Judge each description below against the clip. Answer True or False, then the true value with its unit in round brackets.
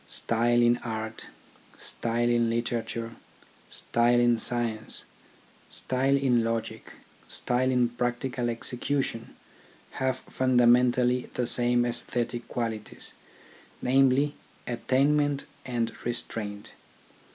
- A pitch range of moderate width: False (1.4 semitones)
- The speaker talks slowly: True (95 wpm)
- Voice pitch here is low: True (120 Hz)